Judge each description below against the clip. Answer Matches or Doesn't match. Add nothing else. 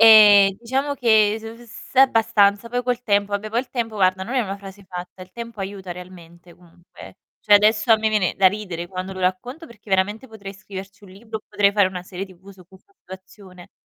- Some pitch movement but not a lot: Matches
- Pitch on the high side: Matches